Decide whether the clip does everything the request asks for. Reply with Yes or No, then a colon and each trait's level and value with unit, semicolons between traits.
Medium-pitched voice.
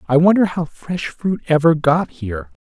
Yes: medium, 155 Hz